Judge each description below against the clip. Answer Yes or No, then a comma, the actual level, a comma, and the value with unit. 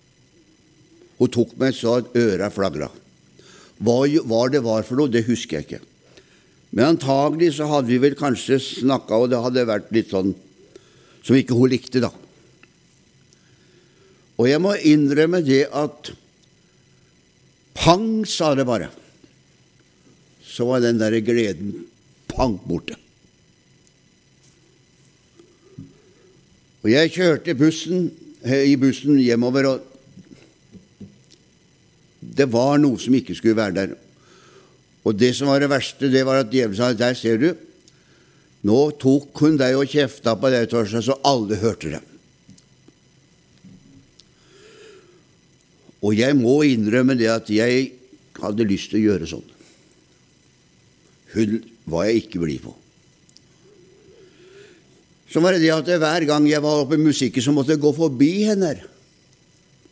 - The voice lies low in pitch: Yes, low, 130 Hz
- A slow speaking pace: Yes, slow, 135 wpm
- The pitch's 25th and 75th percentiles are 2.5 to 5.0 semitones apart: Yes, average, 4.6 semitones